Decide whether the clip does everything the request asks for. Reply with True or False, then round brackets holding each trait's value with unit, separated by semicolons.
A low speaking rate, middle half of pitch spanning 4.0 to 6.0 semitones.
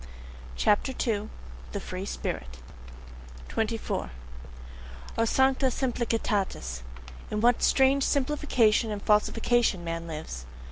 True (95 wpm; 4.8 semitones)